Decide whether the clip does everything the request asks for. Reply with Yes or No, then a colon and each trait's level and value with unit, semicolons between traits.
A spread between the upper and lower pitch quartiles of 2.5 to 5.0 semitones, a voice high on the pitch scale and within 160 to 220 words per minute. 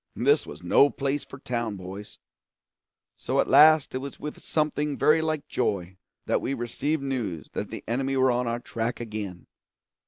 No: average, 4.4 semitones; low, 130 Hz; average, 175 wpm